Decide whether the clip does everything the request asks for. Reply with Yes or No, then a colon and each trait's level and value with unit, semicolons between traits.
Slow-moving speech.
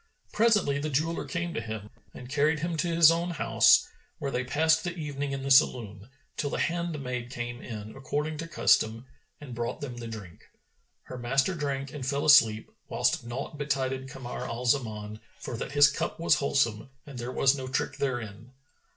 No: average, 185 wpm